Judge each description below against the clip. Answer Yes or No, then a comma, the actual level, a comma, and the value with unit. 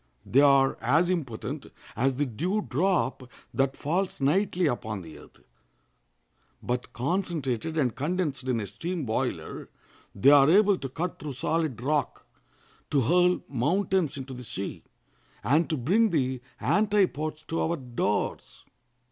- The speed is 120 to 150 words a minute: Yes, average, 140 wpm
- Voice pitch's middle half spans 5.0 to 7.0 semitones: Yes, wide, 5.6 semitones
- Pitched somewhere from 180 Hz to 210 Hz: No, medium, 145 Hz